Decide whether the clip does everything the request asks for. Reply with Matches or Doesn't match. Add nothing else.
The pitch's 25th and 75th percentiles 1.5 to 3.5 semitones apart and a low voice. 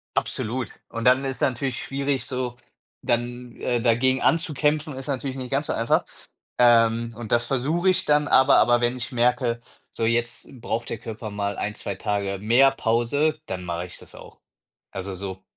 Matches